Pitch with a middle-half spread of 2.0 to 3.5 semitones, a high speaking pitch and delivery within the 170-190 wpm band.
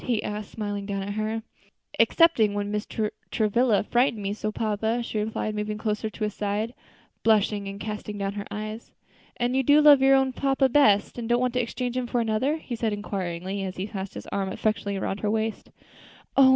No: average, 2.8 semitones; high, 215 Hz; fast, 205 wpm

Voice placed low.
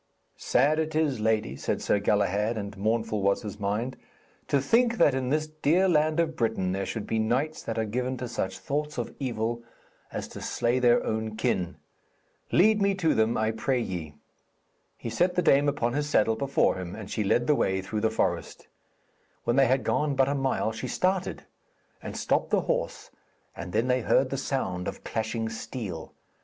Yes: low, 120 Hz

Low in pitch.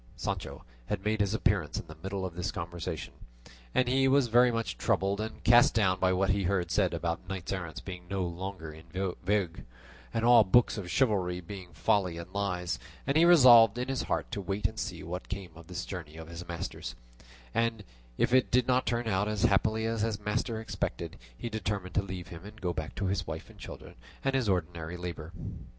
Yes: low, 100 Hz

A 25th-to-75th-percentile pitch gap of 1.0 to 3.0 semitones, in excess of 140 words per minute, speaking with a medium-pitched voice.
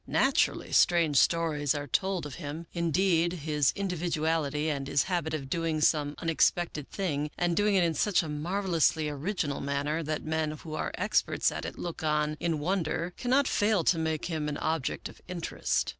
Yes: average, 2.7 semitones; average, 175 wpm; medium, 160 Hz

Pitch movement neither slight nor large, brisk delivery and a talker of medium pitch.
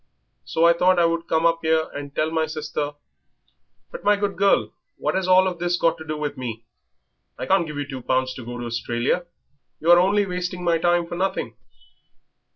Yes: average, 3.5 semitones; fast, 215 wpm; medium, 165 Hz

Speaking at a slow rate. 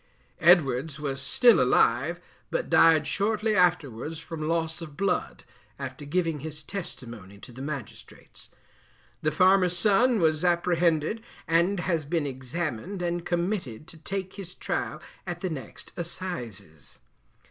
Yes: slow, 130 wpm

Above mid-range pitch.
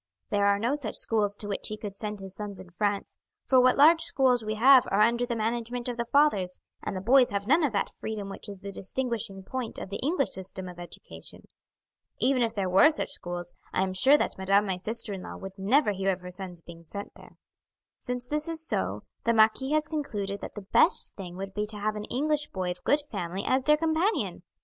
Yes: high, 210 Hz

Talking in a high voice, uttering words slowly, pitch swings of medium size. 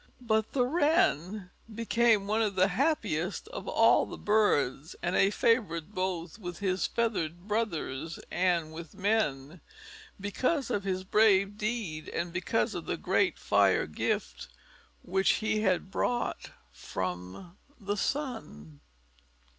Yes: high, 195 Hz; slow, 130 wpm; average, 4.6 semitones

